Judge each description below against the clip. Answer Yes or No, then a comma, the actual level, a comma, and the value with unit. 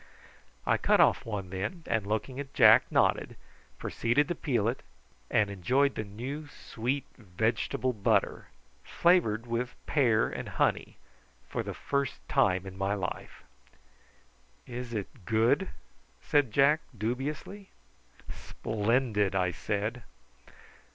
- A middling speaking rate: No, slow, 120 wpm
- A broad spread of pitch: No, average, 4.8 semitones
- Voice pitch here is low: Yes, low, 115 Hz